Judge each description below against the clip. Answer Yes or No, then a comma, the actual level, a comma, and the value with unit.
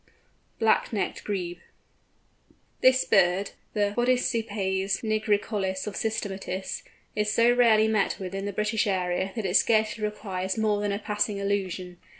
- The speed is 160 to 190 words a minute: No, average, 140 wpm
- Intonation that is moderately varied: No, narrow, 2.3 semitones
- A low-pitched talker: No, high, 205 Hz